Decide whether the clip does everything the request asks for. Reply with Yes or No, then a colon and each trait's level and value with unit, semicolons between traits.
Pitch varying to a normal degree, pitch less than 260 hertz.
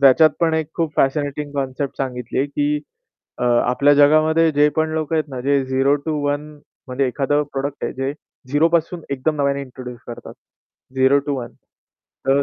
No: narrow, 2.3 semitones; medium, 140 Hz